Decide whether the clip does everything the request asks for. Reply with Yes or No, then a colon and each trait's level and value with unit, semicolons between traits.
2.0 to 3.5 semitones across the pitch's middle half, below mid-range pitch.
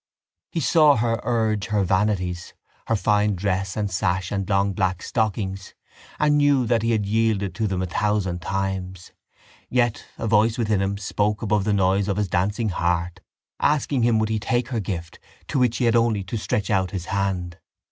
Yes: average, 3.1 semitones; low, 105 Hz